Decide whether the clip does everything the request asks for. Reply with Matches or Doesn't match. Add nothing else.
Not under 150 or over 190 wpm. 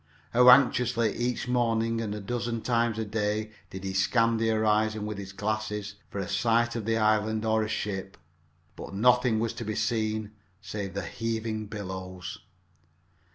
Matches